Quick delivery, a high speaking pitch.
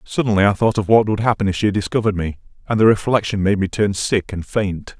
No: fast, 240 wpm; low, 100 Hz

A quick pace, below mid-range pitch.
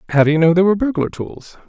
No: fast, 285 wpm; medium, 175 Hz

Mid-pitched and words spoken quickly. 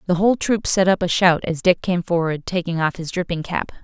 Yes: medium, 175 Hz; fast, 250 wpm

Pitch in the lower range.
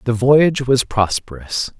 Yes: low, 120 Hz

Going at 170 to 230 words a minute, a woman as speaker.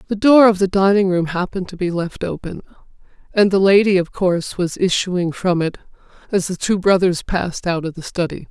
Yes: fast, 205 wpm; female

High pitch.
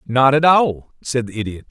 No: low, 130 Hz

